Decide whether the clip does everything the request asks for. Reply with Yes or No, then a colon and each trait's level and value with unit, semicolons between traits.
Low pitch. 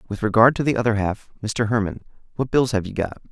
Yes: low, 115 Hz